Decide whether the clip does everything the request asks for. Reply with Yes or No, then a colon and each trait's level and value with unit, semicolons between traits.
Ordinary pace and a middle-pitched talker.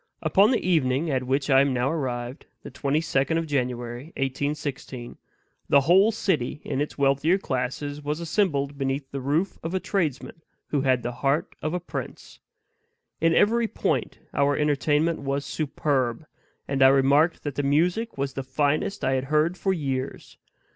Yes: average, 170 wpm; medium, 145 Hz